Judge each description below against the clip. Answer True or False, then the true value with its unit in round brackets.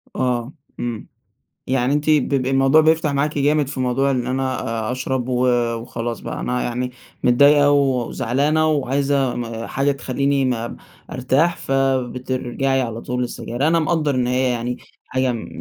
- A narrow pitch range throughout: True (2.3 semitones)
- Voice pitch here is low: True (130 Hz)